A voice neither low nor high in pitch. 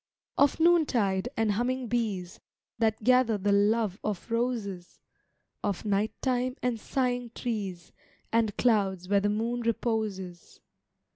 No: high, 220 Hz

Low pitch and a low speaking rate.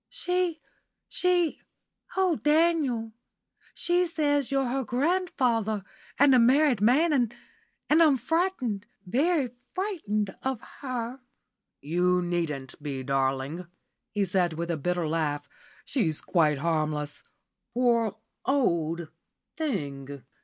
No: high, 230 Hz; slow, 110 wpm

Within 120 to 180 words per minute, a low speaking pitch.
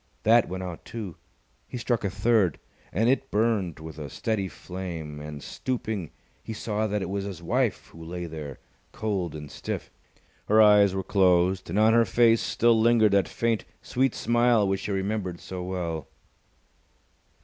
Yes: average, 170 wpm; low, 100 Hz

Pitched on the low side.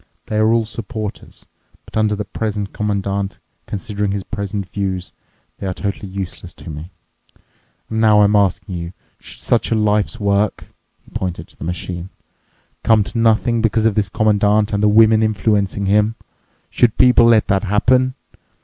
Yes: low, 105 Hz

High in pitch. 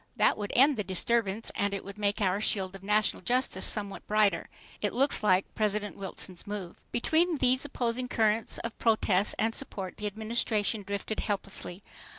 Yes: high, 210 Hz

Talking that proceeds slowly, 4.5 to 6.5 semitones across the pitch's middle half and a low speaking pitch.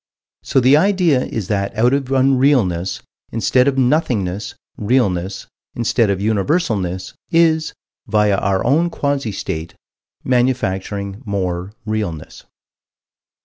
Yes: slow, 105 wpm; wide, 5.6 semitones; low, 110 Hz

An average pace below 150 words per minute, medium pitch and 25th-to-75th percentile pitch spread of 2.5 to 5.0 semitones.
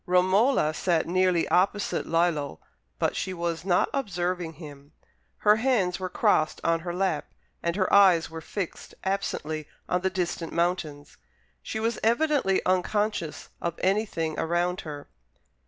Yes: average, 140 wpm; medium, 180 Hz; average, 2.8 semitones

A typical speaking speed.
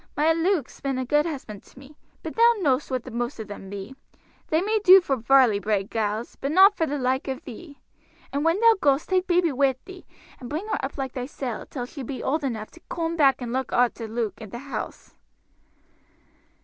No: fast, 215 wpm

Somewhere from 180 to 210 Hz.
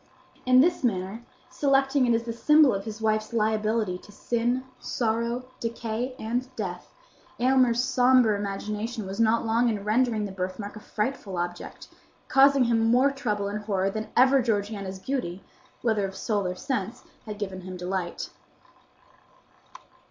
No: high, 220 Hz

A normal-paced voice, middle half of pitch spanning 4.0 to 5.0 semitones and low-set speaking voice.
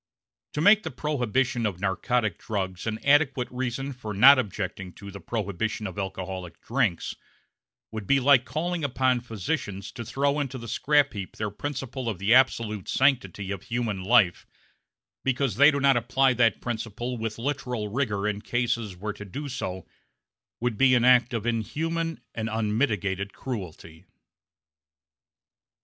Yes: average, 150 wpm; average, 4.6 semitones; low, 115 Hz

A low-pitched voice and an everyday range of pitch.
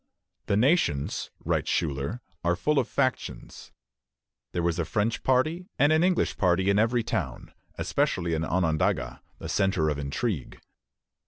No: very low, 95 Hz; wide, 7.7 semitones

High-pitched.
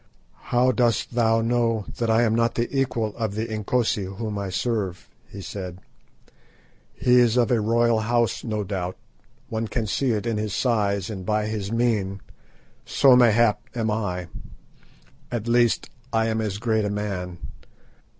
No: low, 110 Hz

